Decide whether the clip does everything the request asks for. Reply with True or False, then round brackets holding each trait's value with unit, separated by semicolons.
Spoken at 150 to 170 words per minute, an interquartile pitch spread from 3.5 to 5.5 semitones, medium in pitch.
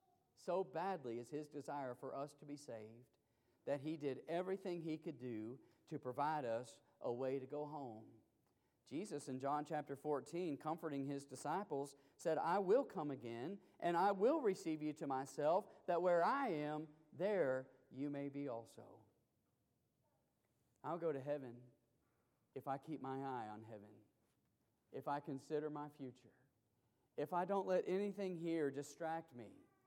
True (155 wpm; 3.8 semitones; 145 Hz)